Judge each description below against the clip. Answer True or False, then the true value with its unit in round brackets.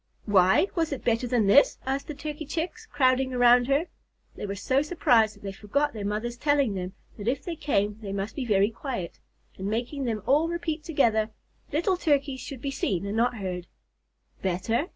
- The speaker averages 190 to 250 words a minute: True (195 wpm)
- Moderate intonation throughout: False (5.7 semitones)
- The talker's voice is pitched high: True (245 Hz)